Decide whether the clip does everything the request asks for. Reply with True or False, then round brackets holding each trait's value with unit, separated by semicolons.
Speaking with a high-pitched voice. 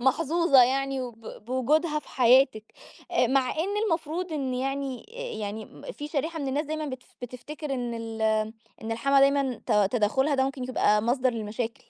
True (265 Hz)